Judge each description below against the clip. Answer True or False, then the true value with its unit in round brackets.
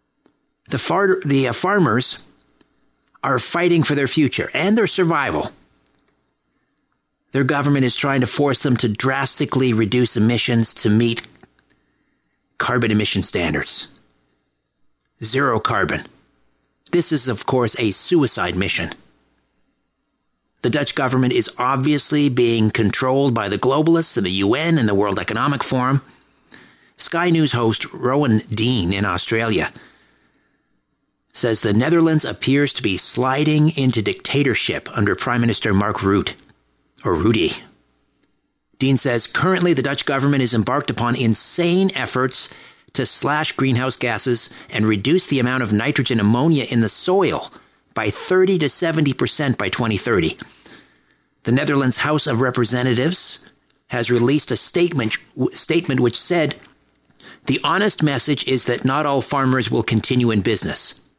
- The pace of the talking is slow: True (130 wpm)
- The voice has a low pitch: True (130 Hz)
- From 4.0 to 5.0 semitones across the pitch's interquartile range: True (4.3 semitones)